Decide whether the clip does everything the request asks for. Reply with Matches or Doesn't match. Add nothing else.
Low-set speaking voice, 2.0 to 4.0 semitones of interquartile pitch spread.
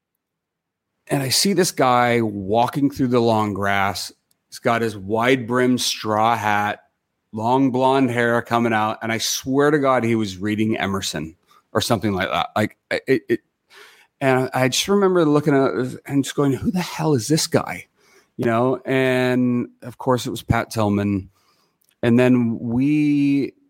Matches